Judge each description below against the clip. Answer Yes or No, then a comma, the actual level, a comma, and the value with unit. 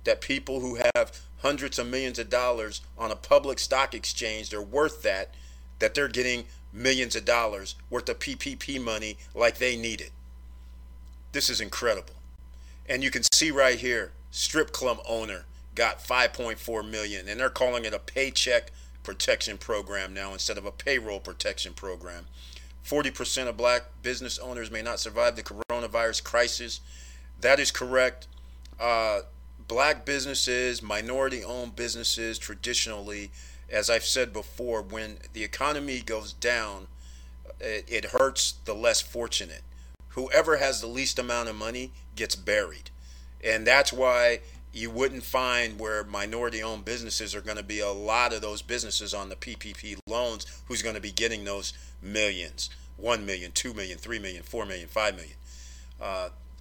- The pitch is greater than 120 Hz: No, low, 110 Hz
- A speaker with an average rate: Yes, average, 155 wpm